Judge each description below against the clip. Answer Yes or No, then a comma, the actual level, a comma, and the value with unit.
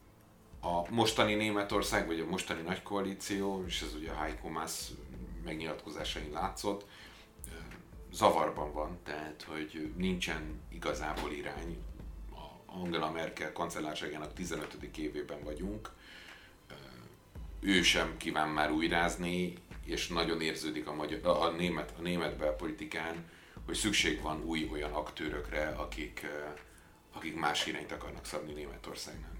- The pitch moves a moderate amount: Yes, average, 3.1 semitones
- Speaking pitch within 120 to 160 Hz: No, very low, 85 Hz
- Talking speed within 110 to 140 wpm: Yes, average, 120 wpm